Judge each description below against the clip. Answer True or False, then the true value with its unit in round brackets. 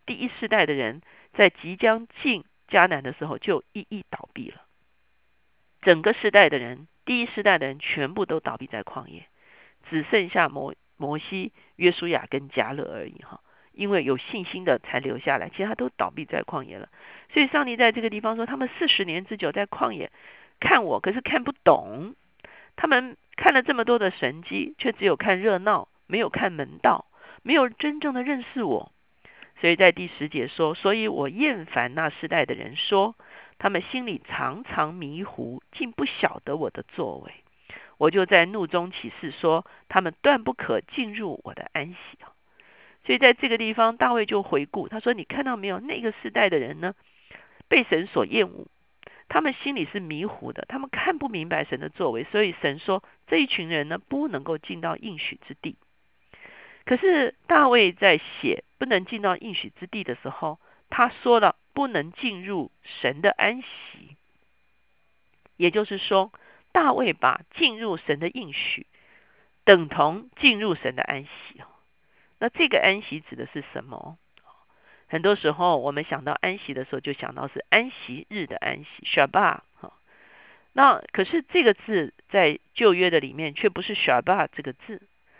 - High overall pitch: True (205 Hz)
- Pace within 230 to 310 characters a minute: True (260 characters per minute)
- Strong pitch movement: True (7.6 semitones)